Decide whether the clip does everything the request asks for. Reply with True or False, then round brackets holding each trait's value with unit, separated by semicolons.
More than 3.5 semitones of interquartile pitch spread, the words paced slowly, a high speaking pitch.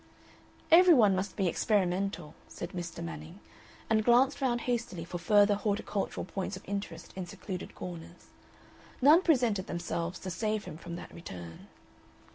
False (4.1 semitones; 145 wpm; 195 Hz)